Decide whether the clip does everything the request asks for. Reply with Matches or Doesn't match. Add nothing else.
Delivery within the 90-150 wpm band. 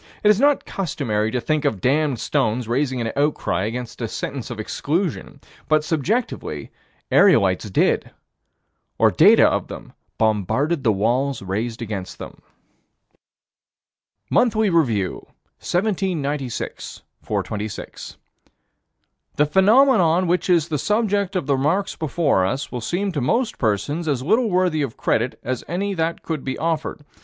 Matches